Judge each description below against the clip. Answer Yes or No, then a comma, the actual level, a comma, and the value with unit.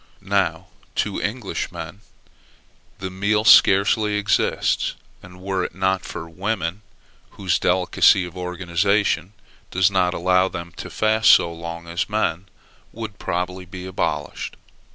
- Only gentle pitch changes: Yes, narrow, 2.2 semitones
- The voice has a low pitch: Yes, very low, 95 Hz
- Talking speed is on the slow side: Yes, slow, 125 wpm